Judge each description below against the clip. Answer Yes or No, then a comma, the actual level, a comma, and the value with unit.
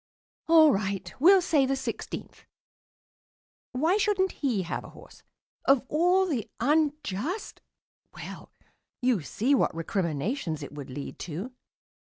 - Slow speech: Yes, slow, 125 wpm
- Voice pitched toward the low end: No, very high, 265 Hz